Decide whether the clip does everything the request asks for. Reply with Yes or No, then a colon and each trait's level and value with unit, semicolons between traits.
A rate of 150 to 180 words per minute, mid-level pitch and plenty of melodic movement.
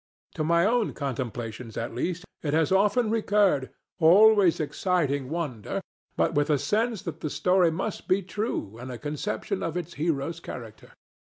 Yes: average, 160 wpm; medium, 165 Hz; wide, 5.9 semitones